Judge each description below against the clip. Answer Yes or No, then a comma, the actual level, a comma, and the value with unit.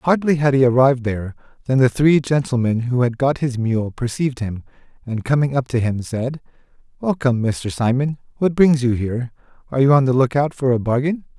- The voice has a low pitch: Yes, low, 130 Hz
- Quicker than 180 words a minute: Yes, average, 200 wpm